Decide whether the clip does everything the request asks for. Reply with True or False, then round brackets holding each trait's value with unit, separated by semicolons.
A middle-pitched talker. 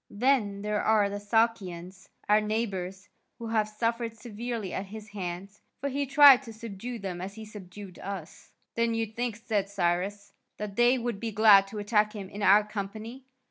False (210 Hz)